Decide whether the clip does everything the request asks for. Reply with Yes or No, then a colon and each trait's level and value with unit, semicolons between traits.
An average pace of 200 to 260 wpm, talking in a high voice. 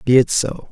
No: fast, 250 wpm; low, 120 Hz